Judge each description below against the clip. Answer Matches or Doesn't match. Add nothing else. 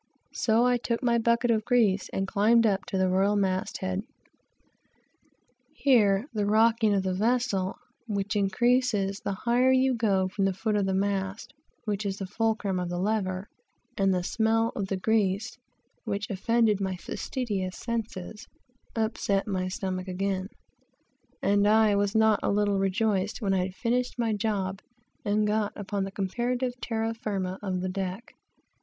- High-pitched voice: Matches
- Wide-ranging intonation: Doesn't match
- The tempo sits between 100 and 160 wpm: Matches